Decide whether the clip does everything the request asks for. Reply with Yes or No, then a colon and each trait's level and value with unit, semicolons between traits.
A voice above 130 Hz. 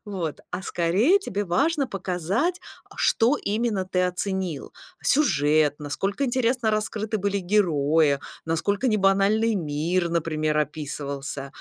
Yes: high, 190 Hz